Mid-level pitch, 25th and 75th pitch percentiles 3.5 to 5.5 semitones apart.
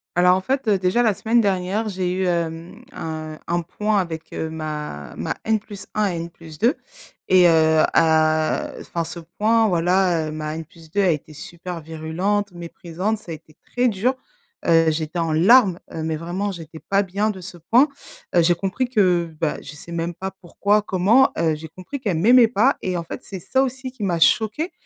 Yes: medium, 180 Hz; average, 4.2 semitones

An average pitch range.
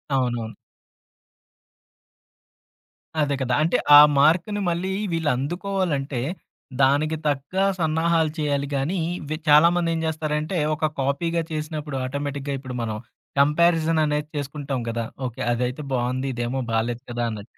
Yes: average, 3.5 semitones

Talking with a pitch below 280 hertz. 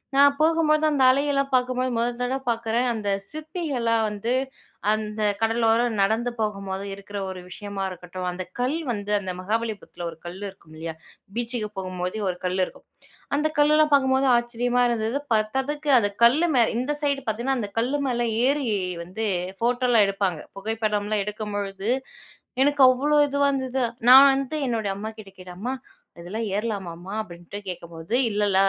Yes: high, 225 Hz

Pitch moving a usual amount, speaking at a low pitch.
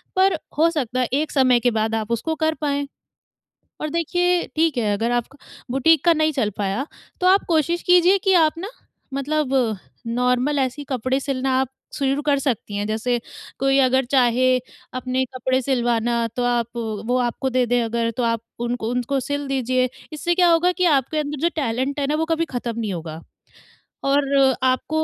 No: average, 4.0 semitones; very high, 265 Hz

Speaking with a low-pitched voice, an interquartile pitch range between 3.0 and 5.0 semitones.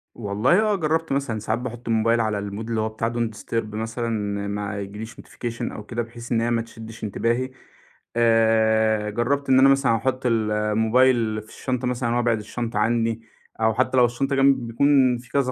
No: low, 115 Hz; narrow, 2.5 semitones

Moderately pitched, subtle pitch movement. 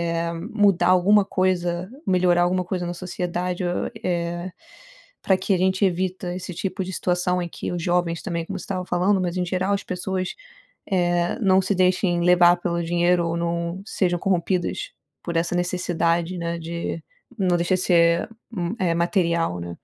Yes: medium, 180 Hz; narrow, 1.4 semitones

